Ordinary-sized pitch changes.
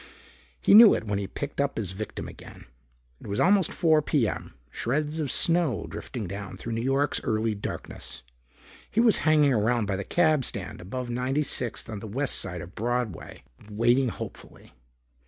No: wide, 6.0 semitones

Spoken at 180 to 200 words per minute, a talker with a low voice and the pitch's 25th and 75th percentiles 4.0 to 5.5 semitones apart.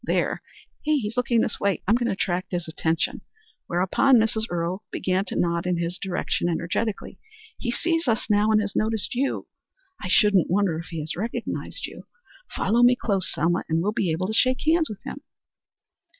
No: average, 185 wpm; high, 200 Hz; average, 4.8 semitones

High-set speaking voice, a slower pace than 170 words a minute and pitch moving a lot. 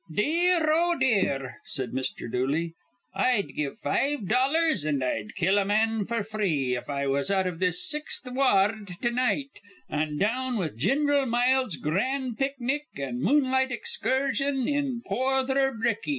Yes: high, 235 Hz; average, 150 wpm; wide, 8.4 semitones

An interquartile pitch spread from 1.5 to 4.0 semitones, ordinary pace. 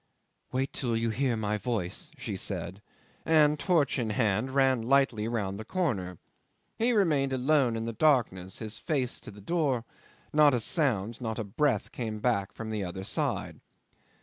No: average, 4.6 semitones; average, 165 wpm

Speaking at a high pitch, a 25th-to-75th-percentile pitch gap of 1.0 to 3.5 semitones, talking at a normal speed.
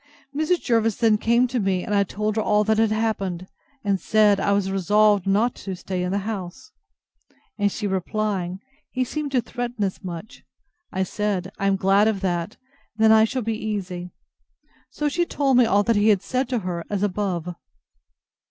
Yes: high, 205 Hz; average, 2.8 semitones; average, 190 wpm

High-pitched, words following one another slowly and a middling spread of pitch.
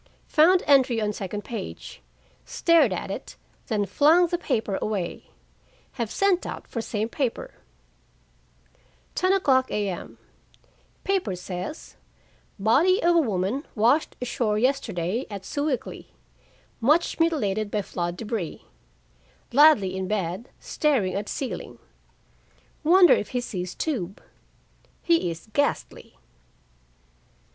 No: high, 230 Hz; slow, 110 wpm; wide, 7.3 semitones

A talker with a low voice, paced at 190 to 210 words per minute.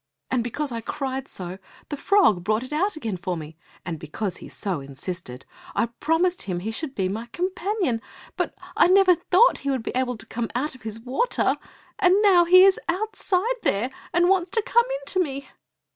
No: very high, 270 Hz; average, 200 wpm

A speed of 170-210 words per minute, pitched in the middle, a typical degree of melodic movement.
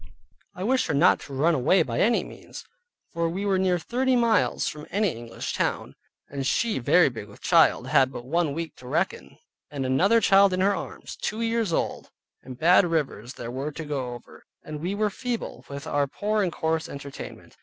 No: fast, 205 wpm; medium, 165 Hz; wide, 6.5 semitones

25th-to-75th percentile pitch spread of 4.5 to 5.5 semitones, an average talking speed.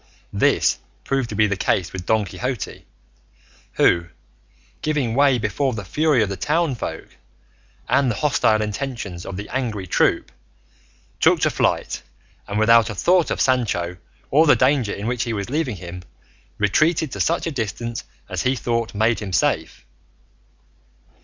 Yes: average, 4.9 semitones; average, 155 wpm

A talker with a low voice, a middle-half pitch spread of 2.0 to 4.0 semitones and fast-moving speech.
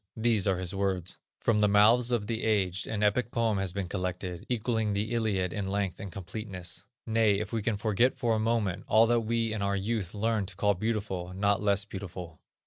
Yes: low, 105 Hz; average, 2.7 semitones; fast, 210 wpm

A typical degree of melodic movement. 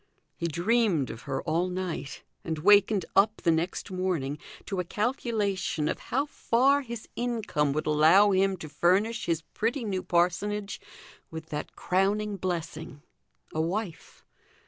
Yes: average, 4.6 semitones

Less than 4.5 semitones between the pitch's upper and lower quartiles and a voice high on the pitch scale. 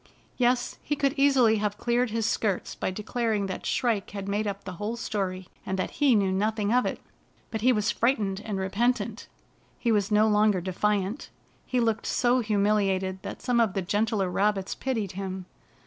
Yes: average, 3.2 semitones; high, 210 Hz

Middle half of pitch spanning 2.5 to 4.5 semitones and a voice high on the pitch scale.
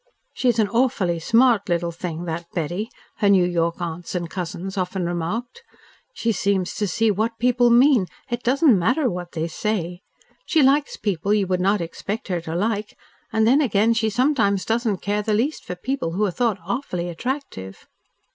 No: average, 5.0 semitones; high, 205 Hz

